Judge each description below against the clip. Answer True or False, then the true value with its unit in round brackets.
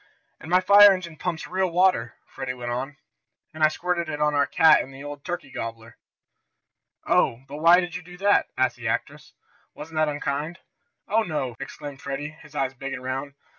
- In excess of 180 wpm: True (200 wpm)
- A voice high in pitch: False (150 Hz)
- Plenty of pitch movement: False (4.6 semitones)